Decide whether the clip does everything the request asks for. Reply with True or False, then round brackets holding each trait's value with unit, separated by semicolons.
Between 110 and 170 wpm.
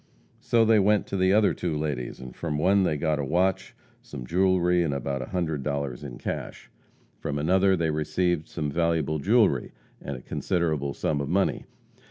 False (185 wpm)